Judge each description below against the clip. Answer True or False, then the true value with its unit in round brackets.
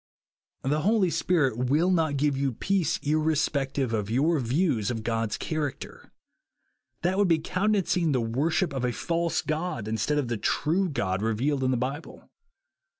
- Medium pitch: True (145 Hz)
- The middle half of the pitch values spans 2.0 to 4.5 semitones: False (5.2 semitones)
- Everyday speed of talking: True (165 wpm)